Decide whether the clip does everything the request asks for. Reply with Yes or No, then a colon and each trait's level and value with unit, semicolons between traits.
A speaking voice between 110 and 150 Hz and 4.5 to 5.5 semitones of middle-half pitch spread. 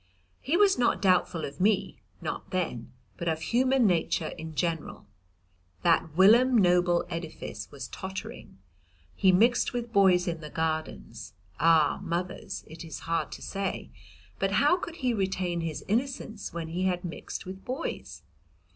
No: medium, 180 Hz; average, 4.8 semitones